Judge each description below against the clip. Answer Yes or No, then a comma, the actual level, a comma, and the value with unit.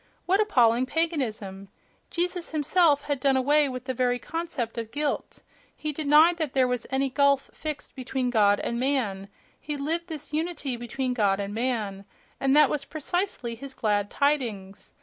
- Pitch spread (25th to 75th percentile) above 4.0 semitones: Yes, average, 4.4 semitones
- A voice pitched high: Yes, very high, 265 Hz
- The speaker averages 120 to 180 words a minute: Yes, average, 165 wpm